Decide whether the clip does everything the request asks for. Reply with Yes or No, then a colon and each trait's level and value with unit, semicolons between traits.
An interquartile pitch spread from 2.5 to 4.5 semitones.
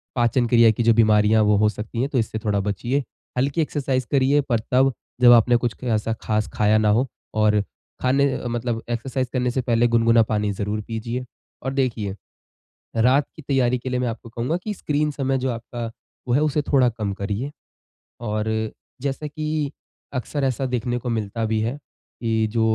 Yes: average, 3.2 semitones